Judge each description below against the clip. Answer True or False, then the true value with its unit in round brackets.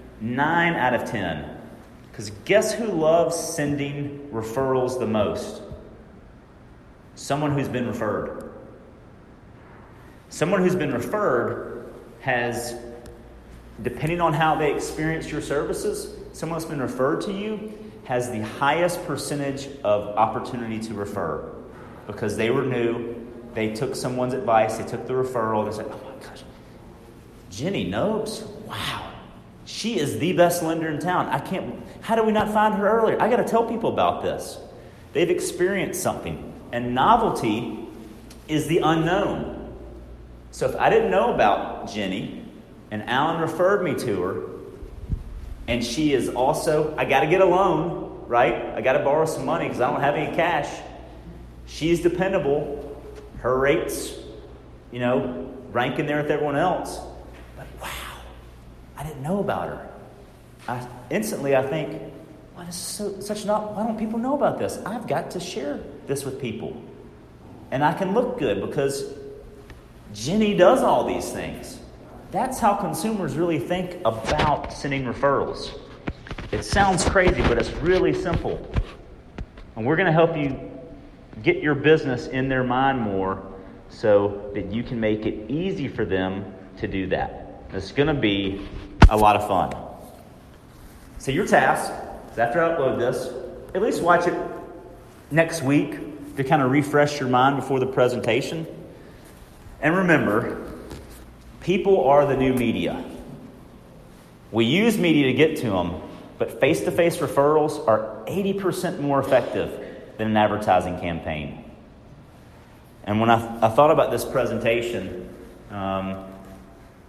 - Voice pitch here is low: True (130 Hz)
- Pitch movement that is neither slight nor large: False (7.3 semitones)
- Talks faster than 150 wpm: False (145 wpm)